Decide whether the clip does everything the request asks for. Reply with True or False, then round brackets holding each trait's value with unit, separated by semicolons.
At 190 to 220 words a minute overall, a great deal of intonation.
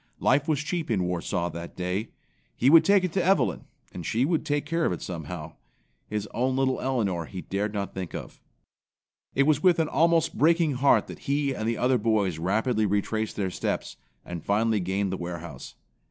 True (195 wpm; 7.7 semitones)